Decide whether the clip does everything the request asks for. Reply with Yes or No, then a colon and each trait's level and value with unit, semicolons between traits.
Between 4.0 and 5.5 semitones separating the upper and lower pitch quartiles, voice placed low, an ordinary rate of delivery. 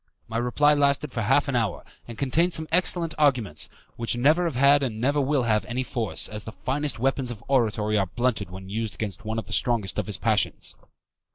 No: average, 4.5 semitones; low, 120 Hz; fast, 210 wpm